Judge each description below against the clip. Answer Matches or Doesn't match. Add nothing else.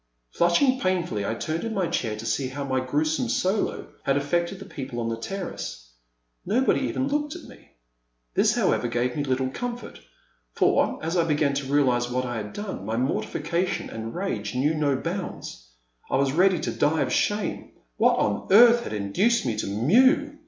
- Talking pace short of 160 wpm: Doesn't match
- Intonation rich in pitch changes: Matches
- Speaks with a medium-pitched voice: Matches